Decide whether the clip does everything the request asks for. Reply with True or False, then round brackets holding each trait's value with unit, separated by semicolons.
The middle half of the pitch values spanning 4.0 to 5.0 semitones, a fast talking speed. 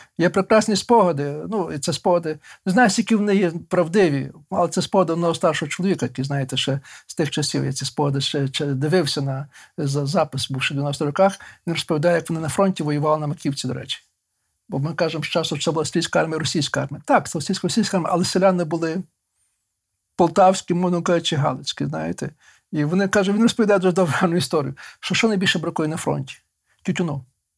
True (4.4 semitones; 190 wpm)